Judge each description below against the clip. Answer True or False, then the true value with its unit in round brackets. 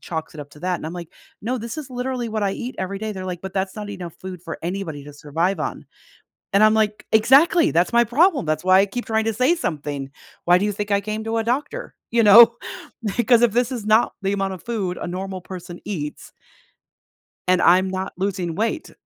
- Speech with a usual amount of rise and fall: True (4.2 semitones)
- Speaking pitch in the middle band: False (200 Hz)